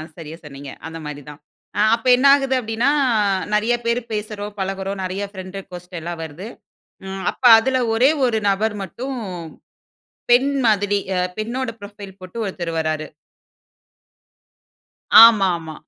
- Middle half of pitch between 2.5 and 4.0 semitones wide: No, average, 4.5 semitones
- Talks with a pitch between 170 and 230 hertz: Yes, high, 200 Hz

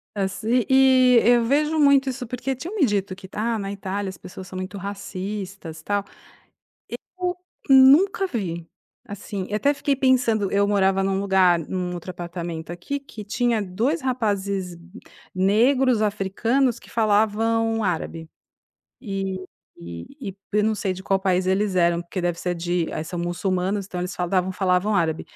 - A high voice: Yes, high, 200 Hz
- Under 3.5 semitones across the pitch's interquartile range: No, average, 4.3 semitones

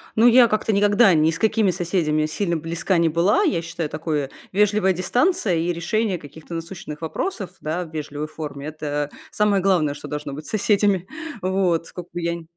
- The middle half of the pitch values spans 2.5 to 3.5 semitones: No, average, 4.4 semitones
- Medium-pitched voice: Yes, medium, 170 Hz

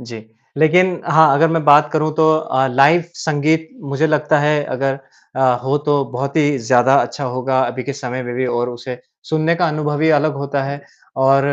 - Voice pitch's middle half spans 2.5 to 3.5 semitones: Yes, average, 3.0 semitones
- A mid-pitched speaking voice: Yes, medium, 145 Hz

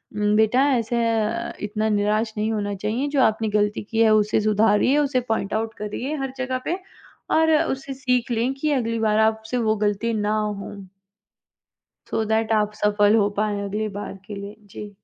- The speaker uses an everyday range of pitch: No, narrow, 1.9 semitones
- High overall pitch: Yes, high, 220 Hz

